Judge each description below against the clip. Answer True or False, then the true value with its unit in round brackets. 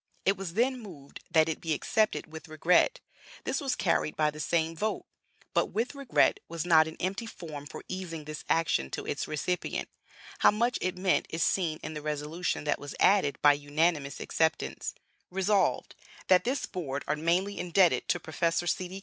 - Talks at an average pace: True (180 wpm)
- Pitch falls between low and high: True (170 Hz)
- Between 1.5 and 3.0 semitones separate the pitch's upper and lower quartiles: False (3.7 semitones)